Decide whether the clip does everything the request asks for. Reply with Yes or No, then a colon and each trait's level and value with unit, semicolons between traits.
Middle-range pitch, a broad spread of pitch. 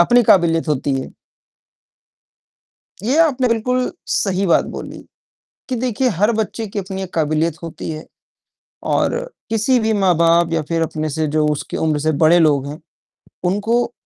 Yes: medium, 180 Hz; wide, 6.0 semitones